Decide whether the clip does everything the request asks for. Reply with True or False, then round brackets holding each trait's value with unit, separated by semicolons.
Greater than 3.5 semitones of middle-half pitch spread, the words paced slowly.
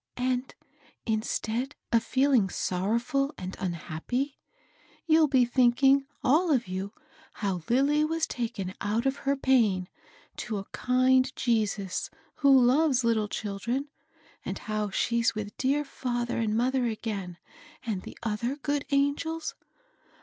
True (4.4 semitones; 130 wpm)